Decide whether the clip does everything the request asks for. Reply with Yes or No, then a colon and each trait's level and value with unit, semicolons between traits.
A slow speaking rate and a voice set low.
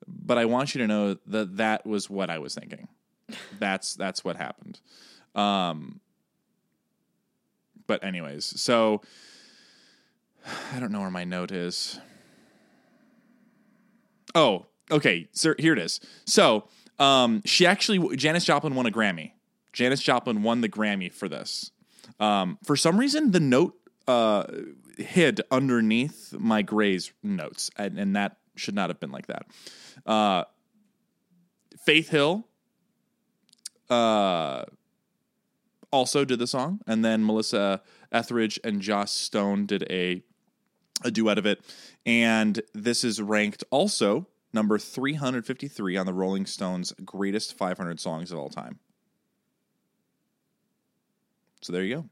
Yes: slow, 130 wpm; low, 120 Hz